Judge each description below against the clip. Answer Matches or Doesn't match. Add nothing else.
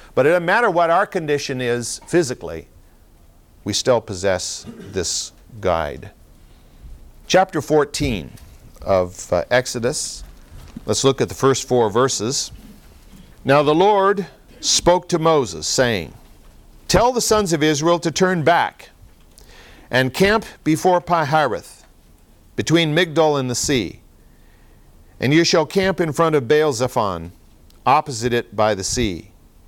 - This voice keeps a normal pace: Doesn't match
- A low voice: Matches